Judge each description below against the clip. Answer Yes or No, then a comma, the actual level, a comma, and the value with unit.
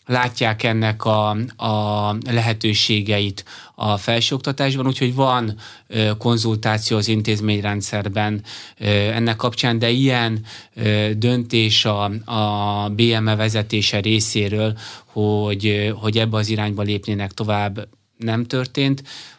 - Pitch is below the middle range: Yes, low, 110 Hz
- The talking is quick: No, slow, 95 wpm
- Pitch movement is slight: Yes, narrow, 1.8 semitones